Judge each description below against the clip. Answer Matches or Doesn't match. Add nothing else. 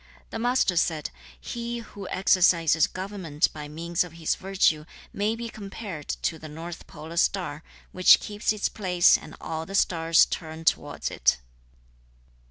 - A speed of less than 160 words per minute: Matches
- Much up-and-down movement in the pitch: Doesn't match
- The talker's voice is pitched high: Doesn't match